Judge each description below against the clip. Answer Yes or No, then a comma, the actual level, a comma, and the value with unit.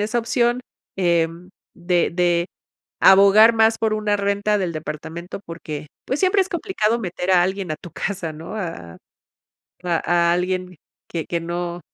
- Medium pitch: Yes, medium, 180 Hz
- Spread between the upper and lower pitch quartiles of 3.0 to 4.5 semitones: Yes, average, 3.8 semitones